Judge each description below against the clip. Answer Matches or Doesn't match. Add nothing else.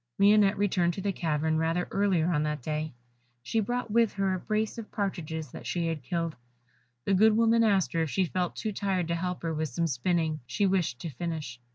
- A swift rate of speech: Matches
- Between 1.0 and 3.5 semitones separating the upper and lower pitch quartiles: Doesn't match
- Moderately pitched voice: Matches